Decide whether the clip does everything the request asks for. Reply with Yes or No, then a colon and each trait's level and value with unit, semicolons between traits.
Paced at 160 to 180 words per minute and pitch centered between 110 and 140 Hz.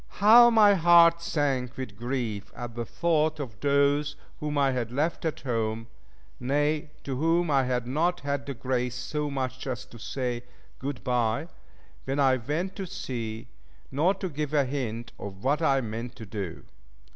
Yes: average, 170 wpm; low, 135 Hz